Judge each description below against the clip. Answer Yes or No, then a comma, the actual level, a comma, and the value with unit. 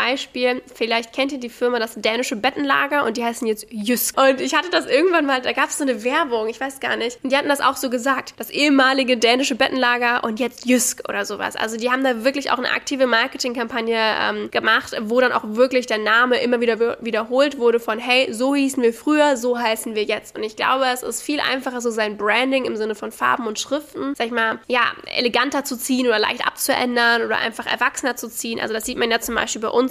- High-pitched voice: Yes, high, 245 Hz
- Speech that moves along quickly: Yes, fast, 235 wpm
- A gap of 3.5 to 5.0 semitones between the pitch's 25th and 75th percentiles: No, narrow, 2.5 semitones